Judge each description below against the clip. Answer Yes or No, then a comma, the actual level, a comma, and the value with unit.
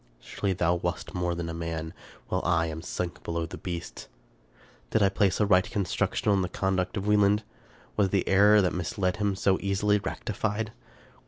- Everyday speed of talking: Yes, average, 180 wpm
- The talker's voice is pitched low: Yes, very low, 95 Hz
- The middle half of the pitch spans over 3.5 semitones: No, average, 2.8 semitones